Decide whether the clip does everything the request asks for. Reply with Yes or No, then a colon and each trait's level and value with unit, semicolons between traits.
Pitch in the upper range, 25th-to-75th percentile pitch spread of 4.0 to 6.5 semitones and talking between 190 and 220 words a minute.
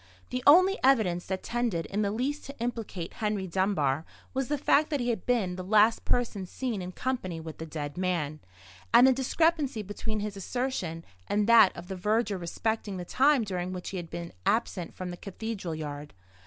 Yes: high, 205 Hz; wide, 5.4 semitones; average, 195 wpm